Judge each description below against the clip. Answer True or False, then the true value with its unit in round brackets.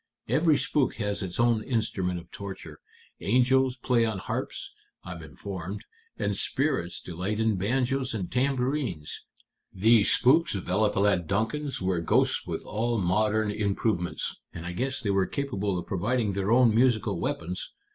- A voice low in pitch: True (105 Hz)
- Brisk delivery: False (145 wpm)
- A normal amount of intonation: True (5.0 semitones)